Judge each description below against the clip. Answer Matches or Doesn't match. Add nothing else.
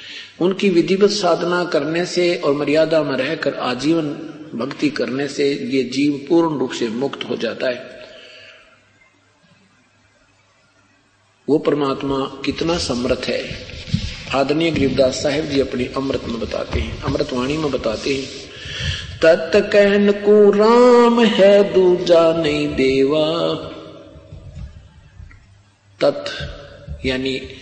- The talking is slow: Matches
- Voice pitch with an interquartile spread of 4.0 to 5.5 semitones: Matches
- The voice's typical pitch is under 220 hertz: Matches